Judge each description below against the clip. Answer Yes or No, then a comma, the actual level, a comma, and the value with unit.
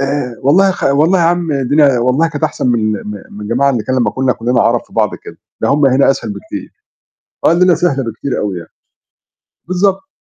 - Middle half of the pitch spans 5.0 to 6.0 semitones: Yes, wide, 5.6 semitones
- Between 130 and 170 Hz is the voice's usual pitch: Yes, medium, 140 Hz